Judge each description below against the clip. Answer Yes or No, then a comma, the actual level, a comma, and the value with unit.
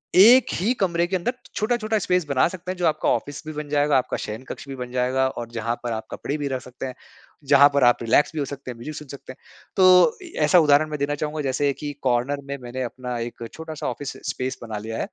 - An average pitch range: Yes, average, 4.2 semitones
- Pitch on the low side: No, medium, 145 Hz